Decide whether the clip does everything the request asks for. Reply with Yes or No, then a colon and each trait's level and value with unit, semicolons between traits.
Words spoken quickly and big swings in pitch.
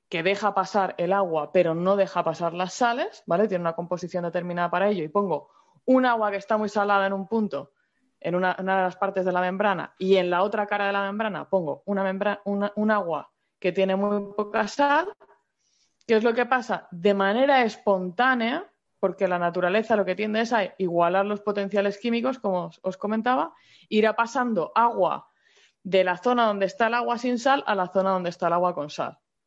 No: fast, 210 wpm; average, 3.4 semitones